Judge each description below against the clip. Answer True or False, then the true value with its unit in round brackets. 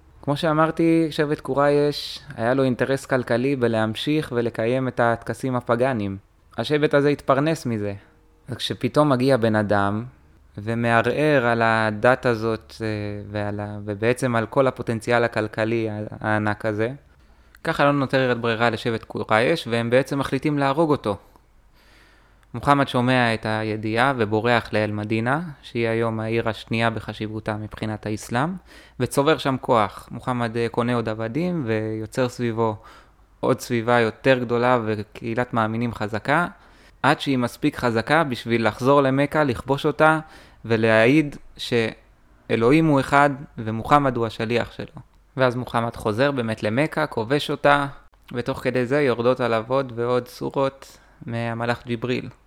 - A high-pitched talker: False (120 Hz)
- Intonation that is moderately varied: True (3.7 semitones)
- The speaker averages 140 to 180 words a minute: False (125 wpm)